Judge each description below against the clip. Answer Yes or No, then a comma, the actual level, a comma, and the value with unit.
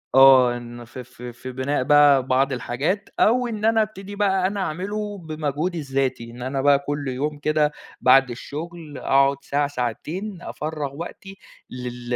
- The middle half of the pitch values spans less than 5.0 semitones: No, wide, 5.5 semitones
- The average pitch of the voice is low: No, medium, 145 Hz